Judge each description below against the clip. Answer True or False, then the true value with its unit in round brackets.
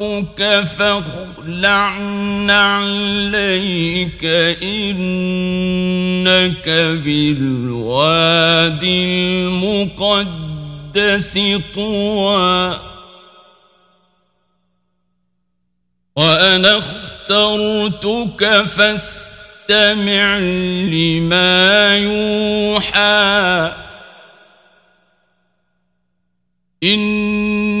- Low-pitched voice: False (185 Hz)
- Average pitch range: True (3.7 semitones)